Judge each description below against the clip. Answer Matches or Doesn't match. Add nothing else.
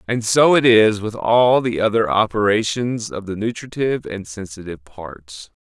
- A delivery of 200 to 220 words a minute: Doesn't match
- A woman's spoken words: Doesn't match